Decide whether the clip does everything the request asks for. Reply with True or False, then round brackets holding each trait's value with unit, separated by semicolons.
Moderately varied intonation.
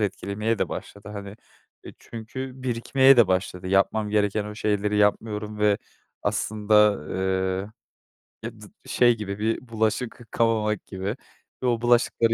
False (2.2 semitones)